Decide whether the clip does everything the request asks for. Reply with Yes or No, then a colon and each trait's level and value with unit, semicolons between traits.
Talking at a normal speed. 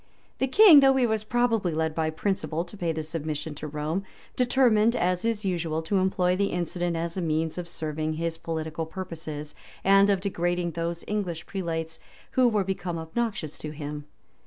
Yes: average, 180 wpm